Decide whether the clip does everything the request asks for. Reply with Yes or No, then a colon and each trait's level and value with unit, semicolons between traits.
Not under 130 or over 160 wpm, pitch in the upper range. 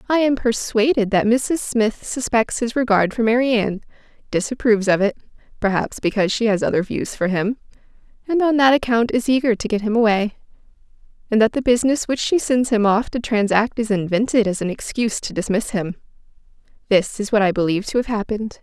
No: average, 185 wpm; high, 225 Hz